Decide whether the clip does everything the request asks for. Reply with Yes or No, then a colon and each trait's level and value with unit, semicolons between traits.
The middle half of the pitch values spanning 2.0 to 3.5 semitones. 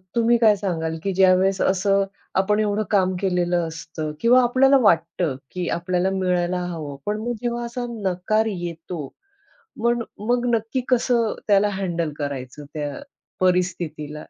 No: average, 4.2 semitones